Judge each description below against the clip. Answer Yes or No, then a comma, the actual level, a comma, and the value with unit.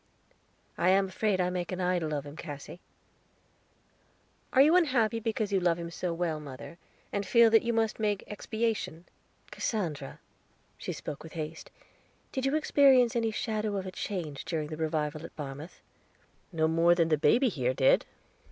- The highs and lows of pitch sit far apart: Yes, wide, 5.8 semitones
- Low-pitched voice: No, medium, 180 Hz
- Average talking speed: Yes, average, 170 wpm